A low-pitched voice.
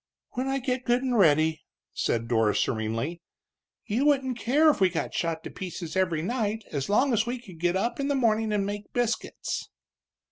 No: high, 210 Hz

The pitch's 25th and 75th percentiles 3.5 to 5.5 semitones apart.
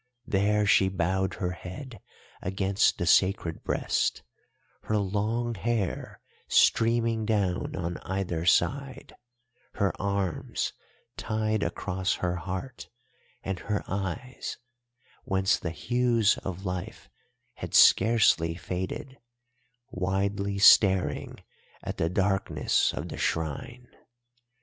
No: average, 3.1 semitones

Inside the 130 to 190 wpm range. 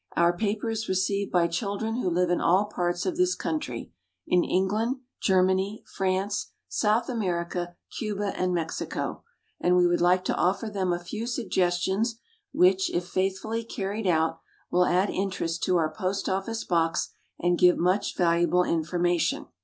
Yes: average, 155 wpm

